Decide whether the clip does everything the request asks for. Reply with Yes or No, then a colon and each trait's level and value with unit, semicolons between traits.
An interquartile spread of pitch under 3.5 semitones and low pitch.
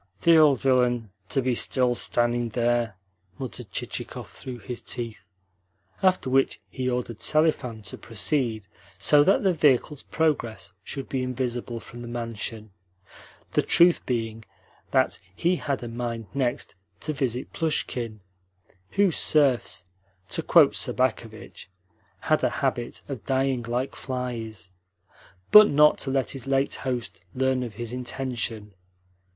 Yes: narrow, 2.6 semitones; low, 125 Hz